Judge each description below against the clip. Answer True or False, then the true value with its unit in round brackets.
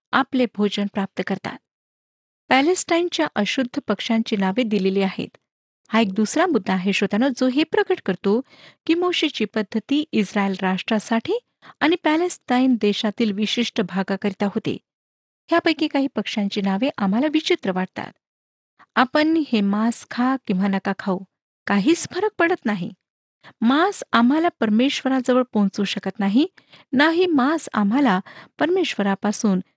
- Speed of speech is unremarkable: True (120 wpm)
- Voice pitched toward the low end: False (230 Hz)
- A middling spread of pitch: False (6.9 semitones)